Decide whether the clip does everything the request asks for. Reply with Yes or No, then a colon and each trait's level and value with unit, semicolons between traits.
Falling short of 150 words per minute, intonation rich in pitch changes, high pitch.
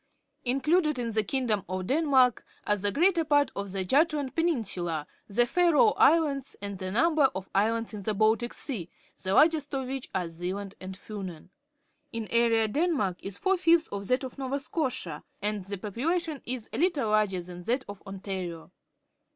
No: average, 175 wpm; wide, 6.6 semitones; high, 230 Hz